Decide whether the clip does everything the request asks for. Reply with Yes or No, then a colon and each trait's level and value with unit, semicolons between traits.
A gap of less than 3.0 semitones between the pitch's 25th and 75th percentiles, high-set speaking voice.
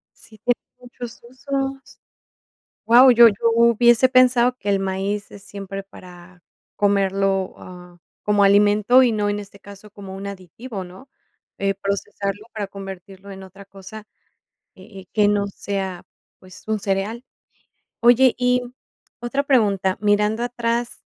No: average, 3.4 semitones; high, 205 Hz